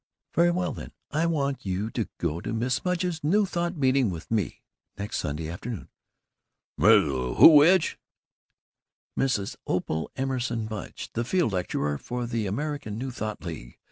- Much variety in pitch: Yes, wide, 7.7 semitones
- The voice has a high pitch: No, low, 120 Hz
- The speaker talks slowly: No, average, 150 wpm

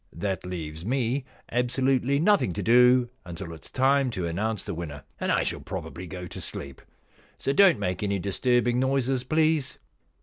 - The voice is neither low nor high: No, low, 120 Hz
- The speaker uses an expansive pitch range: Yes, wide, 6.6 semitones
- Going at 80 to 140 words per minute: No, average, 170 wpm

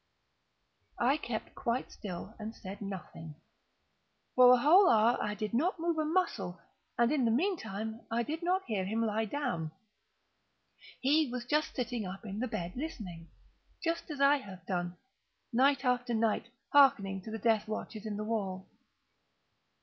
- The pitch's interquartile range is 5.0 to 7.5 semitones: Yes, wide, 5.4 semitones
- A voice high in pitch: Yes, high, 230 Hz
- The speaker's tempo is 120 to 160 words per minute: Yes, average, 155 wpm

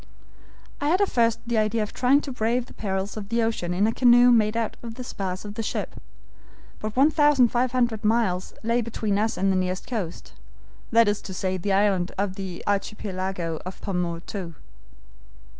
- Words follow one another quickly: No, average, 180 wpm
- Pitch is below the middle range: No, high, 215 Hz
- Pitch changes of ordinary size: Yes, average, 3.7 semitones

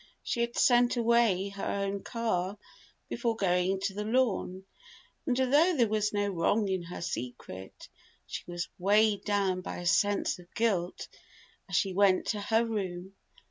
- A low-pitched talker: No, high, 200 Hz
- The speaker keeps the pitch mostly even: No, average, 3.6 semitones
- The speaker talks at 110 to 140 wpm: No, average, 160 wpm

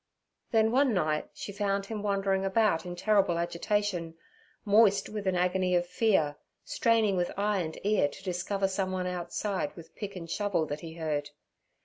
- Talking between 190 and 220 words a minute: No, average, 165 wpm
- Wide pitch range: No, average, 3.0 semitones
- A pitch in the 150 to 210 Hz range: Yes, high, 190 Hz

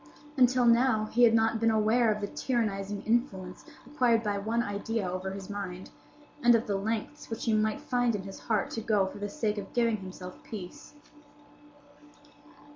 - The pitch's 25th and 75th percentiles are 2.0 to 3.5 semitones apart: Yes, average, 2.7 semitones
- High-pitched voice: Yes, high, 215 Hz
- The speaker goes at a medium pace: Yes, average, 180 wpm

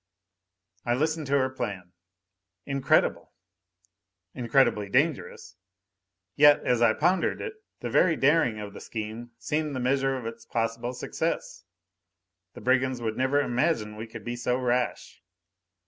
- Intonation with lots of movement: No, average, 3.6 semitones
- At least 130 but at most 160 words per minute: Yes, slow, 135 wpm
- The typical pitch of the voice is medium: No, low, 125 Hz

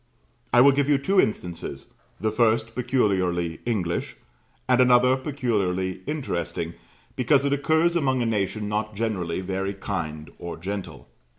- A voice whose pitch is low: Yes, low, 110 Hz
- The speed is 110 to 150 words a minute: Yes, slow, 135 wpm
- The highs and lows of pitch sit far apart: Yes, wide, 5.9 semitones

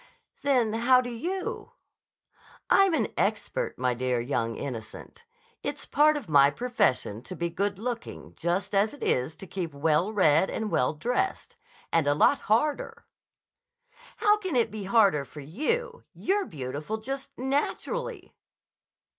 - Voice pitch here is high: Yes, high, 215 Hz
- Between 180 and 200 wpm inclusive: No, average, 145 wpm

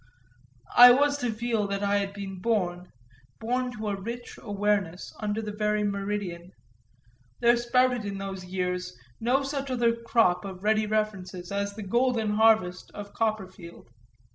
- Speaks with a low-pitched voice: No, high, 210 Hz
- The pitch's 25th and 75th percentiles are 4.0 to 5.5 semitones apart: No, average, 3.2 semitones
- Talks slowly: No, average, 150 wpm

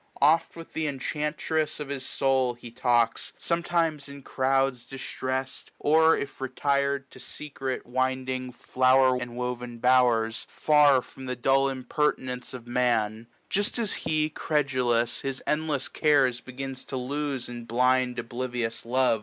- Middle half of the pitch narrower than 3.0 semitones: Yes, narrow, 2.4 semitones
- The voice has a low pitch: Yes, low, 130 Hz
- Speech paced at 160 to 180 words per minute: No, average, 140 wpm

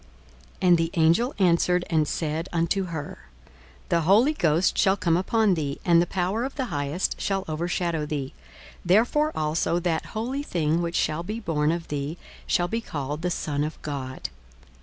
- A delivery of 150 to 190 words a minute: Yes, average, 175 wpm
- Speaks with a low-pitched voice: No, medium, 170 Hz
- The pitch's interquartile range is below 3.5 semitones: No, average, 3.8 semitones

